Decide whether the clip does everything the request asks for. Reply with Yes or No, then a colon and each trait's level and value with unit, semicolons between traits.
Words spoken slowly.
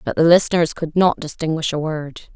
No: fast, 205 wpm